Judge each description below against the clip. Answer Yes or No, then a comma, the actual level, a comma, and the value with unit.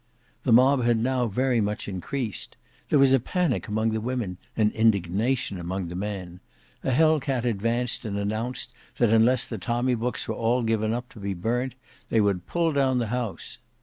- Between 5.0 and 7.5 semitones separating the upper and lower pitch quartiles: No, average, 3.3 semitones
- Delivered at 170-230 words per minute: Yes, average, 185 wpm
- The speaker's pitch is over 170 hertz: No, low, 115 Hz